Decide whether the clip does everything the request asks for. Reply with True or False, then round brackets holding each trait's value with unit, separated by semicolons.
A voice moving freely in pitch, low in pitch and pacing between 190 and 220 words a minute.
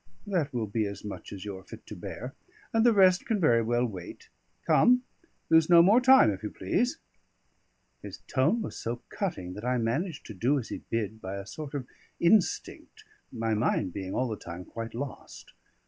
True (8.6 semitones; 120 Hz; 195 wpm)